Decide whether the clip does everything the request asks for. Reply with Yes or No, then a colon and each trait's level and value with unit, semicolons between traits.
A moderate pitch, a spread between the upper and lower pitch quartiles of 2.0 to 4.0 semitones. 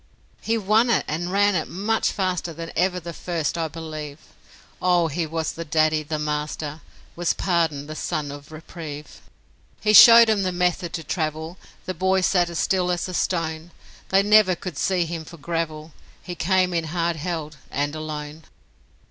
Yes: medium, 170 Hz; average, 2.8 semitones